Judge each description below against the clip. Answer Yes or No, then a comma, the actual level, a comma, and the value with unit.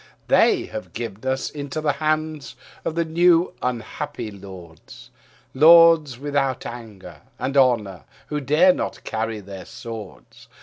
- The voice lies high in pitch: No, low, 130 Hz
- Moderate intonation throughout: No, wide, 5.9 semitones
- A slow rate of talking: Yes, slow, 125 wpm